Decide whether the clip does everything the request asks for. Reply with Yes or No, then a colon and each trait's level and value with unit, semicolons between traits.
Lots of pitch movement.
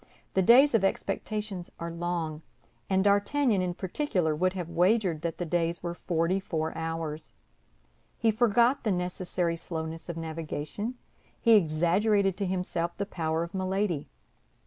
No: average, 3.4 semitones